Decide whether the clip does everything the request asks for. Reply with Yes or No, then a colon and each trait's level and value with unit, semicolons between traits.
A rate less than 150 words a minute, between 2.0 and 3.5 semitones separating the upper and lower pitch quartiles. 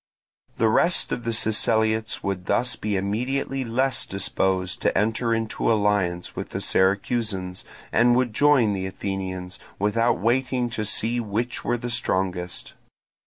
No: average, 140 wpm; average, 3.9 semitones